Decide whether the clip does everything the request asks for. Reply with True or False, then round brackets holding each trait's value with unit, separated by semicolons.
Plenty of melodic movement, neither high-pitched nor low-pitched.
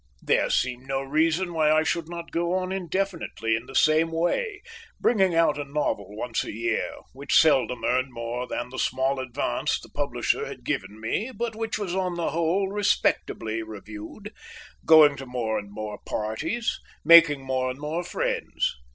True (6.1 semitones; 150 Hz)